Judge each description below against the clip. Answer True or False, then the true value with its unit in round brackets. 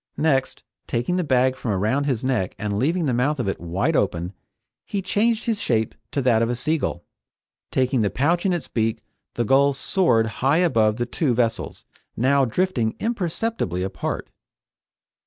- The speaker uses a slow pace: False (175 wpm)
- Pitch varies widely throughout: True (6.2 semitones)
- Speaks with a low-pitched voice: True (130 Hz)